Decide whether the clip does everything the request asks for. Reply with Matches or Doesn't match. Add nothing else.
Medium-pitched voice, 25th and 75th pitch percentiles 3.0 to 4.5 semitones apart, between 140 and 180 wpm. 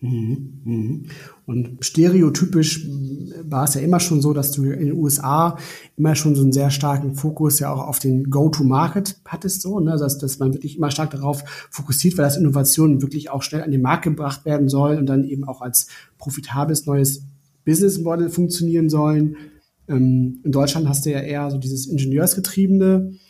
Doesn't match